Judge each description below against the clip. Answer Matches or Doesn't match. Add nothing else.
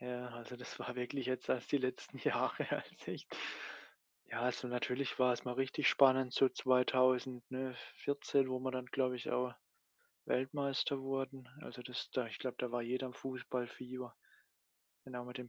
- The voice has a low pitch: Matches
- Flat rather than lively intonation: Matches